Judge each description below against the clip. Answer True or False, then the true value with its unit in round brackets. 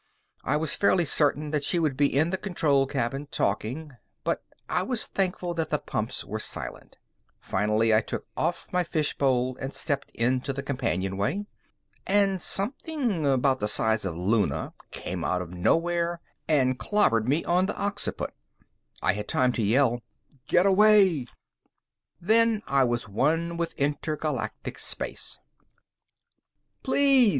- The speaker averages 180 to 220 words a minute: False (145 wpm)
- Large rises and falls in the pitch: True (6.8 semitones)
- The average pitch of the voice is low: False (145 Hz)